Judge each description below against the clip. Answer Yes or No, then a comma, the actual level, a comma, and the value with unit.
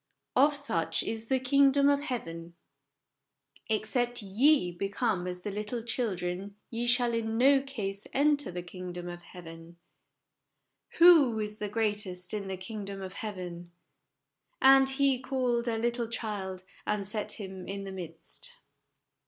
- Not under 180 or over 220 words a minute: No, average, 155 wpm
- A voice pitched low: No, high, 215 Hz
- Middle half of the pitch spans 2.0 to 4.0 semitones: No, average, 5.2 semitones